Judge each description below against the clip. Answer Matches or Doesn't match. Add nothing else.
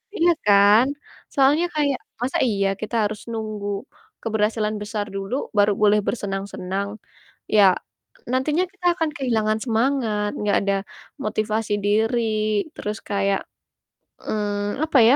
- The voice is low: Doesn't match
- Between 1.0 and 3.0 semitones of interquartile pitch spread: Doesn't match